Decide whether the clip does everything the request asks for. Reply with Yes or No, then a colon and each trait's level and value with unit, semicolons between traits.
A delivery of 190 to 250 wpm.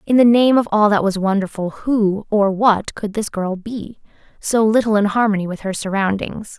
Yes: average, 200 wpm